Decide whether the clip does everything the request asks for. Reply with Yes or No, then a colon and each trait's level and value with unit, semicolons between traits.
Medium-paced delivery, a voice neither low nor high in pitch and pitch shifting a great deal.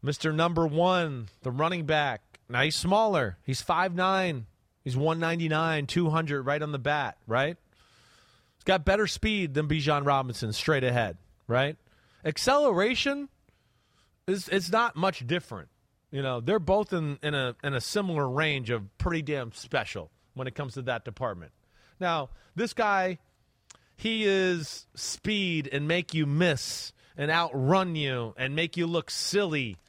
Yes: average, 155 wpm; medium, 150 Hz; wide, 5.7 semitones